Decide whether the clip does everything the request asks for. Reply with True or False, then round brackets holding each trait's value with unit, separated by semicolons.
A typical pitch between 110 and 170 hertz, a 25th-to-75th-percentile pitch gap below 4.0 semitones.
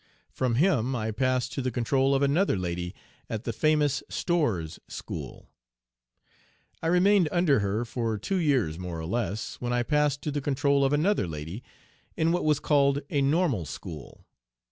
False (135 Hz; 5.5 semitones)